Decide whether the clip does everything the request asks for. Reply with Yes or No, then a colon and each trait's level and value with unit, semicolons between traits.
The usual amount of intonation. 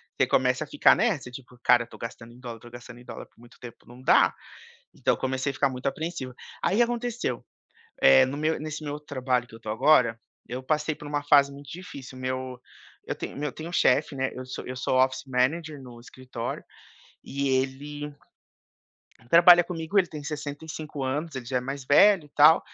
Yes: average, 3.4 semitones